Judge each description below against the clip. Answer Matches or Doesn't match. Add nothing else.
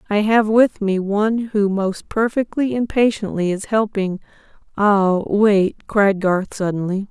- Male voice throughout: Doesn't match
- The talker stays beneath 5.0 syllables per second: Matches